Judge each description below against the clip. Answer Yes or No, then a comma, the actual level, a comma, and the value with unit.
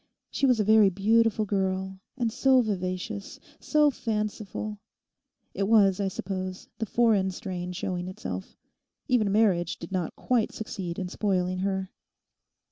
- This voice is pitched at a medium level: No, high, 195 Hz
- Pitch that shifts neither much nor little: Yes, average, 3.0 semitones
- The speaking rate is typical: No, slow, 130 wpm